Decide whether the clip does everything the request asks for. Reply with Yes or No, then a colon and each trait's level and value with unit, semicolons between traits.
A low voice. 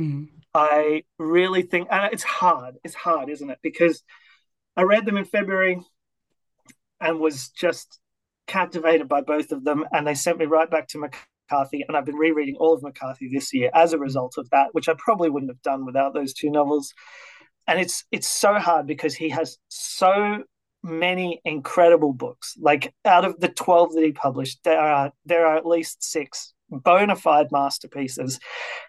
No: medium, 160 Hz